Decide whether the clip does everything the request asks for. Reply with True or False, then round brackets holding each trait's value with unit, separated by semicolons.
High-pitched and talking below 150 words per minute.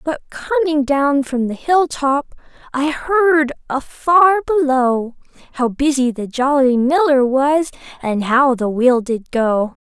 True (275 Hz; 140 wpm)